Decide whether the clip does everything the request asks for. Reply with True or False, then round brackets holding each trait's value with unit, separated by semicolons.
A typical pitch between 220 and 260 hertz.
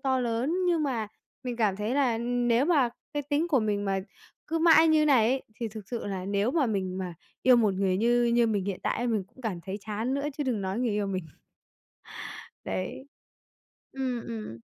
True (235 Hz)